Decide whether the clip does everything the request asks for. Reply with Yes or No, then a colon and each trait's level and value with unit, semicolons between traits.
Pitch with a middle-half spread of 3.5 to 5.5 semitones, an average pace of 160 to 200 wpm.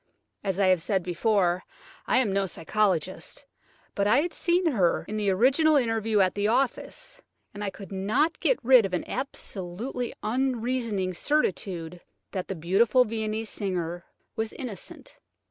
No: average, 5.0 semitones; average, 150 wpm